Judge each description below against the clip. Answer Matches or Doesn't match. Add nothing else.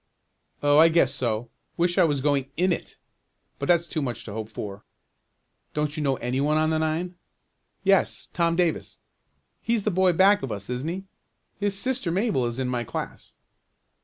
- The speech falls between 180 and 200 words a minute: Matches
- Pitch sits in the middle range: Matches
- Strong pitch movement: Matches